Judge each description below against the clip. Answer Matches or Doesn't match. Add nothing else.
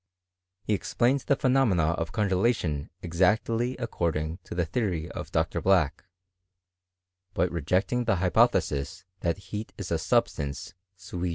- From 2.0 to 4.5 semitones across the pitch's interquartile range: Doesn't match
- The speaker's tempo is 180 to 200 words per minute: Doesn't match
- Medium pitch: Doesn't match